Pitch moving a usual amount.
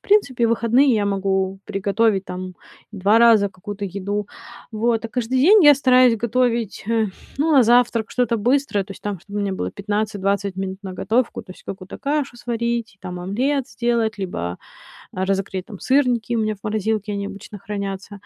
Yes: average, 3.3 semitones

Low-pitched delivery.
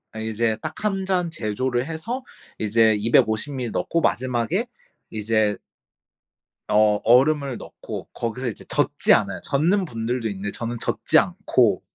Yes: low, 120 Hz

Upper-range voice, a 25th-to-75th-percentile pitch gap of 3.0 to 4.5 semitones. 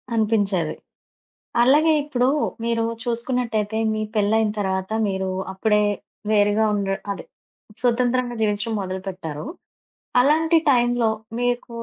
Yes: high, 220 Hz; average, 3.3 semitones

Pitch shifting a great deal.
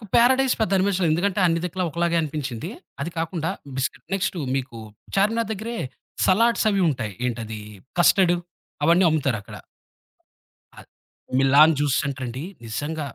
Yes: wide, 6.0 semitones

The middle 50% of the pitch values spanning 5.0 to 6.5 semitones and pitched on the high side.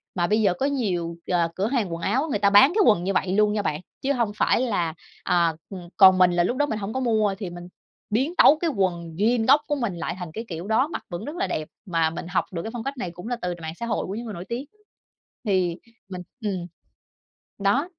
Yes: average, 5.3 semitones; high, 200 Hz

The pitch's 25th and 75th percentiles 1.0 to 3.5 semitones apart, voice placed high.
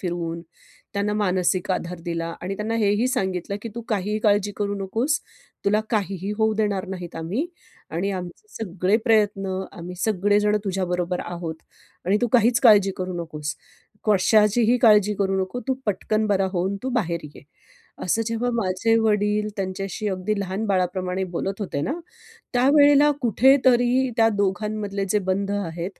Yes: average, 2.9 semitones; high, 200 Hz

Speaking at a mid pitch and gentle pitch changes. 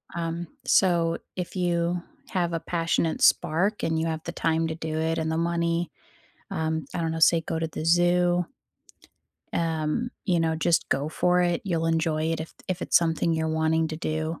Yes: medium, 165 Hz; narrow, 1.3 semitones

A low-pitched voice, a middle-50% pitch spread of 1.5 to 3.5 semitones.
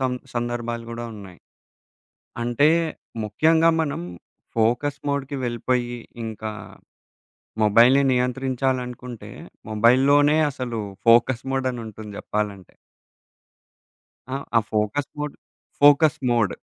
Yes: low, 120 Hz; average, 3.1 semitones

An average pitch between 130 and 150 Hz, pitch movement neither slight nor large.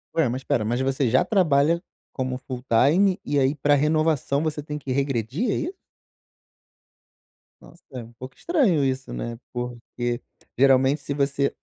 Yes: medium, 140 Hz; average, 3.3 semitones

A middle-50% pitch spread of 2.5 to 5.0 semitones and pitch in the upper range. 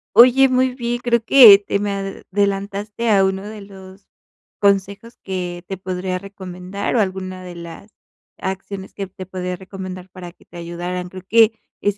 No: narrow, 2.0 semitones; high, 195 Hz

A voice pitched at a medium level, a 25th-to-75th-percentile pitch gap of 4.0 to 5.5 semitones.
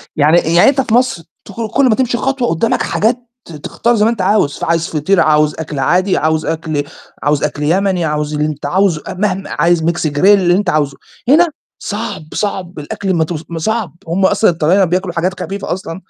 Yes: medium, 175 Hz; average, 4.8 semitones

